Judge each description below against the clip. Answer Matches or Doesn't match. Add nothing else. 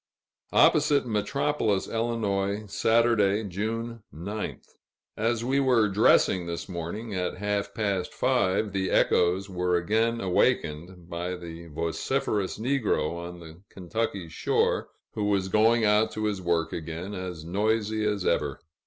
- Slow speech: Matches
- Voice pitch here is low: Matches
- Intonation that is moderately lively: Matches